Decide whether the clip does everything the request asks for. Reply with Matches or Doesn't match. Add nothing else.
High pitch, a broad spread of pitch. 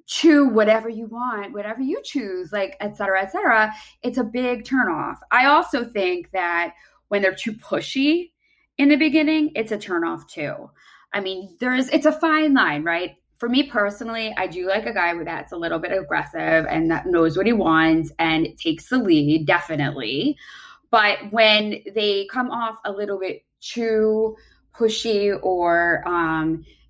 Matches